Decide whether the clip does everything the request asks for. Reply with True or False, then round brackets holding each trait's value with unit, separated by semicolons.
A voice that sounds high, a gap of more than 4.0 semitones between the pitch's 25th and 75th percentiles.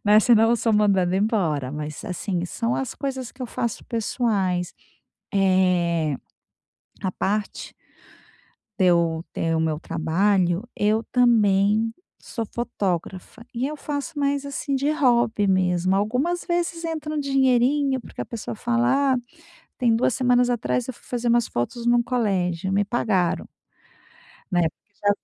True (220 Hz; 5.1 semitones)